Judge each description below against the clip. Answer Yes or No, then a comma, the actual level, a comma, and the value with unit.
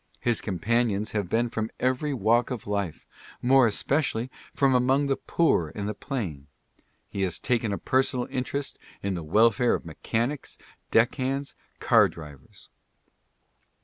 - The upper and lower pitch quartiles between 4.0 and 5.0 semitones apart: Yes, average, 4.5 semitones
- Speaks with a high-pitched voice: No, low, 115 Hz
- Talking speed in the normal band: Yes, average, 150 wpm